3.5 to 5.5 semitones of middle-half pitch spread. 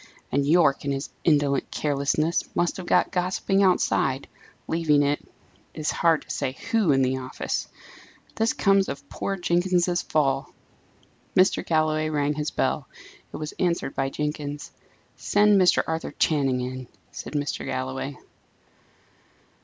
Yes: average, 3.9 semitones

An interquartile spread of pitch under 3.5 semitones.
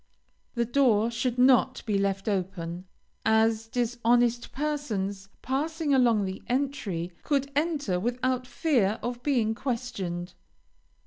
No: average, 4.6 semitones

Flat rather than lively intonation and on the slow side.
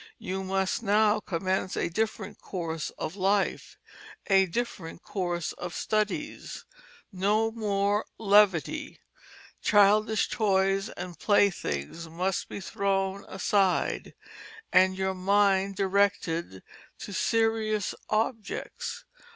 Yes: narrow, 2.1 semitones; slow, 100 wpm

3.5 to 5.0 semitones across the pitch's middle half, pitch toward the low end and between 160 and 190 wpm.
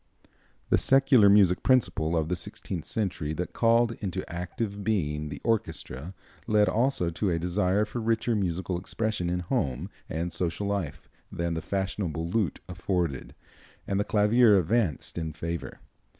No: average, 4.1 semitones; very low, 95 Hz; average, 150 wpm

